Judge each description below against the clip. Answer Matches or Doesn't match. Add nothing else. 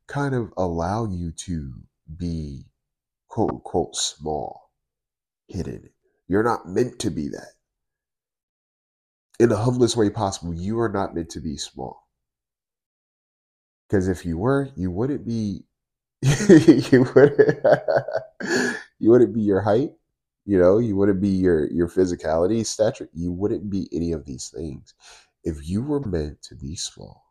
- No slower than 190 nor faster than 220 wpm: Doesn't match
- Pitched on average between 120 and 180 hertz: Doesn't match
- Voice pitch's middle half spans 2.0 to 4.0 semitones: Doesn't match